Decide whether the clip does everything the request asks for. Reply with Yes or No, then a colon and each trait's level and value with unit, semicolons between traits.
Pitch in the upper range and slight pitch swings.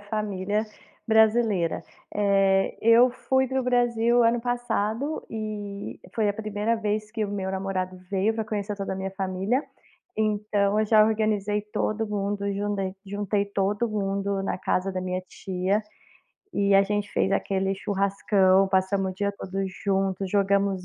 Yes: high, 205 Hz; narrow, 1.8 semitones